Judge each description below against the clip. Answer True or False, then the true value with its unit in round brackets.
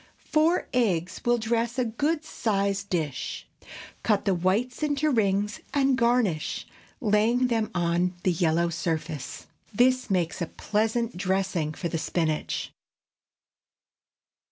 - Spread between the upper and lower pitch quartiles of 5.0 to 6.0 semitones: True (5.6 semitones)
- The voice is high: True (205 Hz)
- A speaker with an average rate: False (120 wpm)